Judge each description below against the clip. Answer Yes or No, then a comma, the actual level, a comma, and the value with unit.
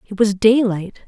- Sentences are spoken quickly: No, average, 170 wpm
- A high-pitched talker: Yes, high, 210 Hz